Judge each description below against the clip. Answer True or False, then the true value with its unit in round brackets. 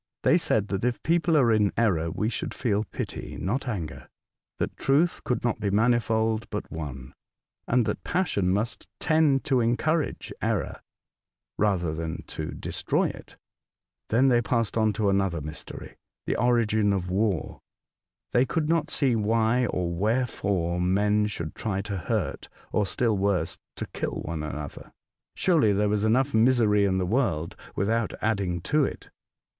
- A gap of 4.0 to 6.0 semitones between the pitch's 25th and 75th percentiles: True (4.3 semitones)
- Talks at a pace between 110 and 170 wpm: True (160 wpm)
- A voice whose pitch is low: True (110 Hz)